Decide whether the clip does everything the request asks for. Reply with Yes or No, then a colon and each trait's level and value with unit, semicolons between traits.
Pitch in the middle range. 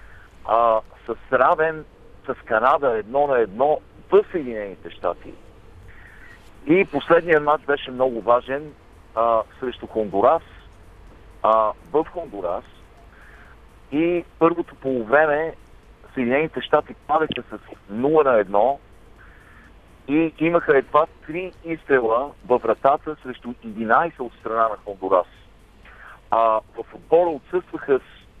No: low, 130 Hz